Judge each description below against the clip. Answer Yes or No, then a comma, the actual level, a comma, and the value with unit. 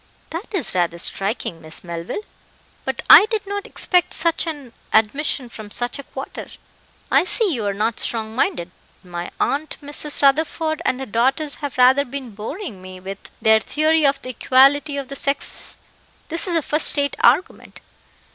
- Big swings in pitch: Yes, wide, 6.1 semitones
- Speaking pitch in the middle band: No, very high, 275 Hz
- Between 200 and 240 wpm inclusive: No, average, 170 wpm